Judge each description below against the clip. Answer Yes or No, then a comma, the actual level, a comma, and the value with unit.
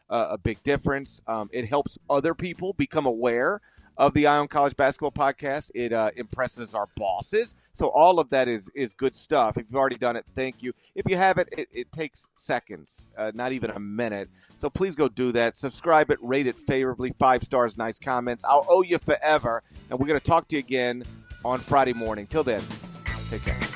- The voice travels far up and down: No, average, 3.5 semitones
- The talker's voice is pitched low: Yes, low, 130 Hz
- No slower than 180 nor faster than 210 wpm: Yes, fast, 205 wpm